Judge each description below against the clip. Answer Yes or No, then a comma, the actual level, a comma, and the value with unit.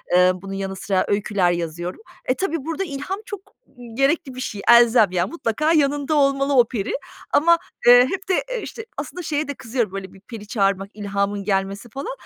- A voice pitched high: Yes, high, 240 Hz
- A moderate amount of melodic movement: No, wide, 6.7 semitones